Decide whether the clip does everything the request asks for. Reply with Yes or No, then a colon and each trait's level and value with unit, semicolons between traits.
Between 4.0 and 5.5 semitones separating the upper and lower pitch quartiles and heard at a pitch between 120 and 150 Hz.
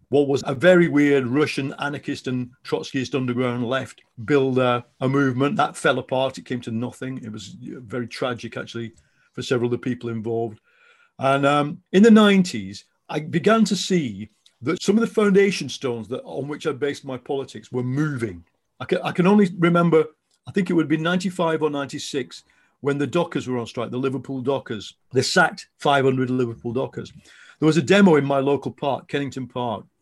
Yes: average, 4.3 semitones; medium, 140 Hz